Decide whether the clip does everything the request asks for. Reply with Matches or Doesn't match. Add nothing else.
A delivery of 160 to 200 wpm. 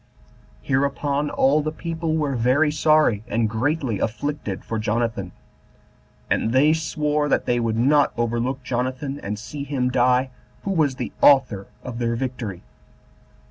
Doesn't match